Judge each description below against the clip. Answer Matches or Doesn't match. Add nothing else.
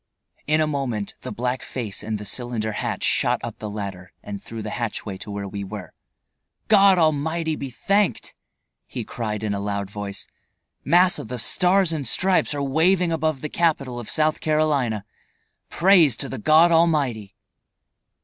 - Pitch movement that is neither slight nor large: Doesn't match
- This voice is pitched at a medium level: Doesn't match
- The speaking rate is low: Doesn't match